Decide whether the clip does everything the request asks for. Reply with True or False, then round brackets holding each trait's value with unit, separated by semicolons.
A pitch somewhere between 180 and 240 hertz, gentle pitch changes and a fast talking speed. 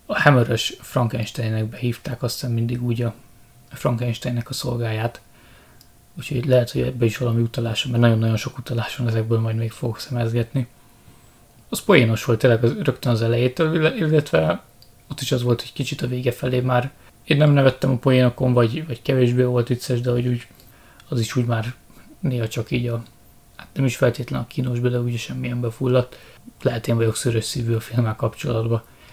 False (120 Hz; 1.6 semitones; 175 wpm)